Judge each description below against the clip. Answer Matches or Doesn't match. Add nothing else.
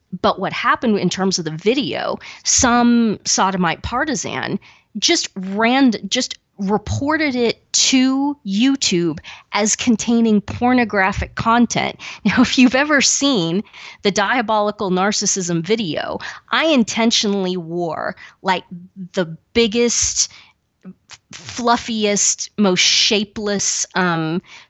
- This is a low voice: Doesn't match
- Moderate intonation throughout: Matches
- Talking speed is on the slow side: Matches